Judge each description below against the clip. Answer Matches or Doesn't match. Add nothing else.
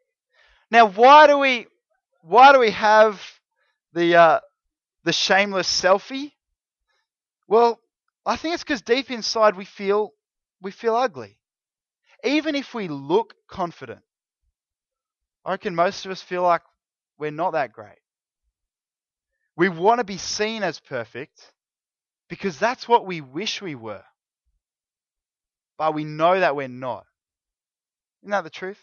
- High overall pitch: Matches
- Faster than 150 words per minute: Doesn't match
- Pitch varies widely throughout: Matches